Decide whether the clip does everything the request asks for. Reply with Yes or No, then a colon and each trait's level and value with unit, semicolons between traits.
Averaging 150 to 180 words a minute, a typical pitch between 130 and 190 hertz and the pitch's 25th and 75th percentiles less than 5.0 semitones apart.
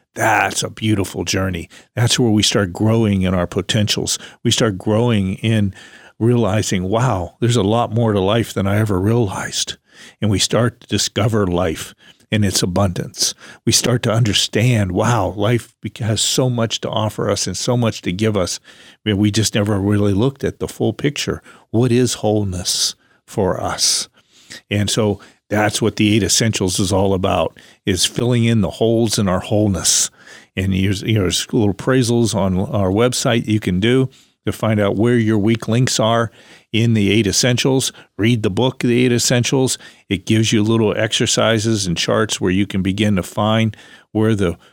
No: average, 175 wpm; low, 110 Hz; average, 2.9 semitones